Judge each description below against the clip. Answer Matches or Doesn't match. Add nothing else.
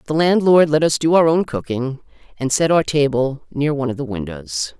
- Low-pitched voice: Doesn't match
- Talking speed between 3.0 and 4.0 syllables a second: Doesn't match